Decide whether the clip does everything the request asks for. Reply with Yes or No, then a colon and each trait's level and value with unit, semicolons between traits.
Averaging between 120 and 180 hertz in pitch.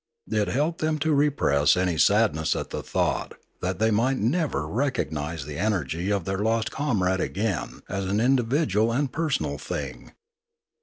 No: low, 110 Hz